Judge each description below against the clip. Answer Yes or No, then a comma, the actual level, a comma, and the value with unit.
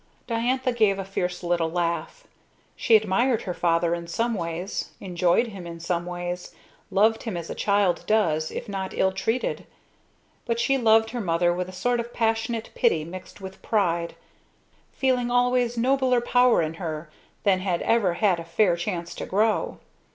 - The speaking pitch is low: No, high, 195 Hz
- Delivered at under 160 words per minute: No, average, 170 wpm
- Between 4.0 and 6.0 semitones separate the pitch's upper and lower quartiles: Yes, average, 5.1 semitones